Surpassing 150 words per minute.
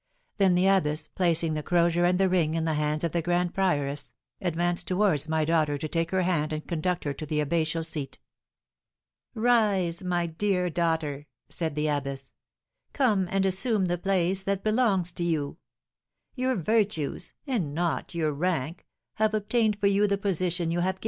Yes: average, 175 wpm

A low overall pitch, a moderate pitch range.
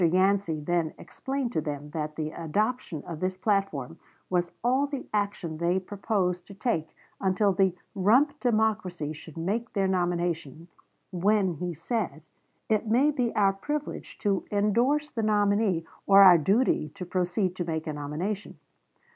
No: high, 190 Hz; average, 4.3 semitones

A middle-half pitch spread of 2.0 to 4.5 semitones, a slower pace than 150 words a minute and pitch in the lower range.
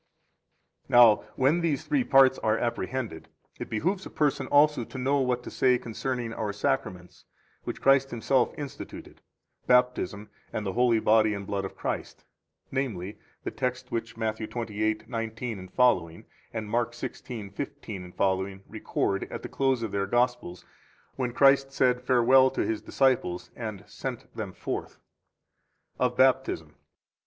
Yes: average, 3.6 semitones; average, 140 wpm; low, 120 Hz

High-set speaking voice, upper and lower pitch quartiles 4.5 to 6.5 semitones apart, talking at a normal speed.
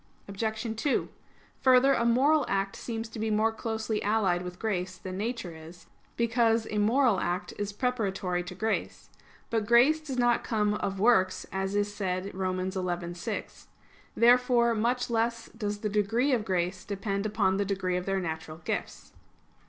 No: high, 210 Hz; average, 3.6 semitones; average, 160 wpm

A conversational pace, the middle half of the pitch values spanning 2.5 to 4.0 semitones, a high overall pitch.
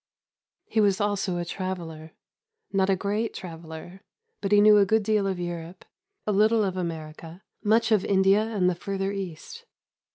Yes: average, 165 wpm; average, 3.0 semitones; high, 195 Hz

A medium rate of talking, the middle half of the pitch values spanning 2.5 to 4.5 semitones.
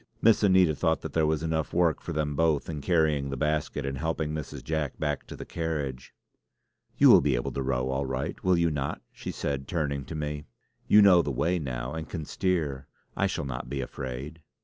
No: fast, 215 wpm; average, 3.0 semitones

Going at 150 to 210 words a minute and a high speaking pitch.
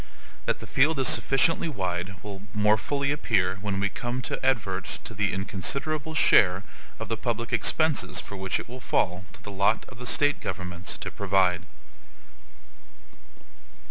No: average, 160 wpm; low, 105 Hz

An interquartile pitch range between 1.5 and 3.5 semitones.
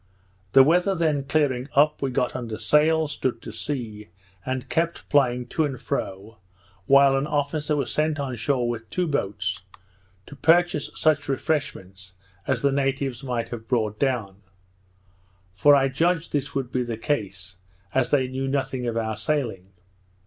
No: average, 4.1 semitones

